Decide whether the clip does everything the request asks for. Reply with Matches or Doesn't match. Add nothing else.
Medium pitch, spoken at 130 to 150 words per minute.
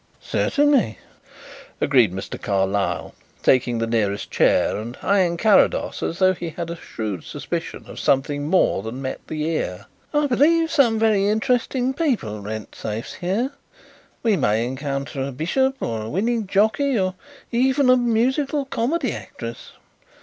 Matches